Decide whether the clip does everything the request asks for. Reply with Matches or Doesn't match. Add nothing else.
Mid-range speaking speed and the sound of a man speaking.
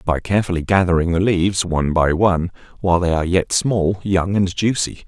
Matches